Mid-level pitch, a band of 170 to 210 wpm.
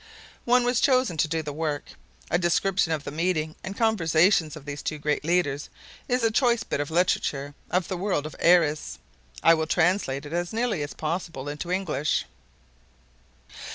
Yes: medium, 165 Hz; average, 175 wpm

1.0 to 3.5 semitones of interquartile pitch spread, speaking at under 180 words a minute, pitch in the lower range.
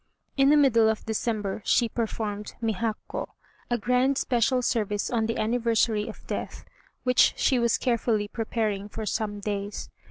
No: narrow, 2.4 semitones; average, 150 wpm; high, 225 Hz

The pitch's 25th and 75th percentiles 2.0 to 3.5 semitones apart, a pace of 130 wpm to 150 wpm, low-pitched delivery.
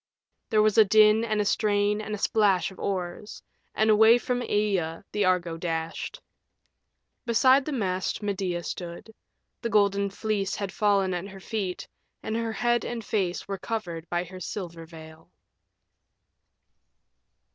No: average, 3.2 semitones; average, 145 wpm; high, 200 Hz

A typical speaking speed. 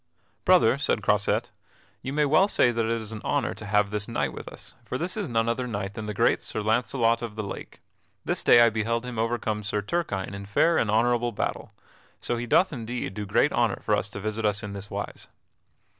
No: fast, 220 wpm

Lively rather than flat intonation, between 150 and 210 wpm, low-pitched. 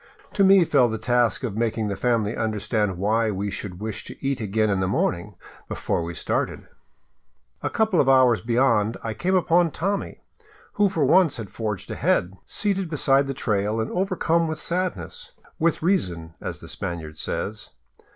Yes: wide, 8.2 semitones; average, 170 wpm; low, 115 Hz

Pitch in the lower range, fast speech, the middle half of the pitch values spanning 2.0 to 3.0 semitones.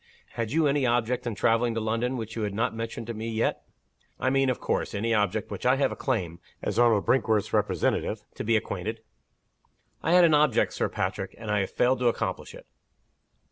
Yes: low, 115 Hz; fast, 215 wpm; average, 2.7 semitones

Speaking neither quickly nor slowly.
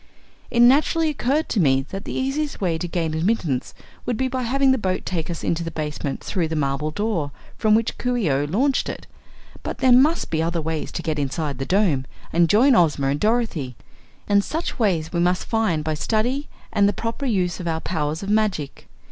No: fast, 210 wpm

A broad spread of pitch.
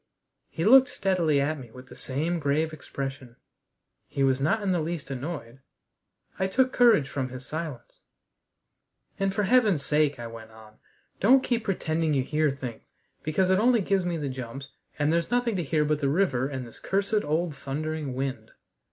Yes: wide, 5.8 semitones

